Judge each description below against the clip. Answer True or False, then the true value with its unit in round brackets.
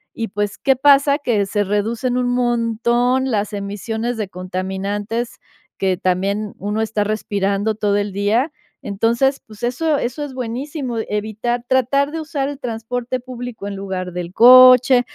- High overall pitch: True (225 Hz)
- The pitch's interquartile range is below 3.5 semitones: False (3.8 semitones)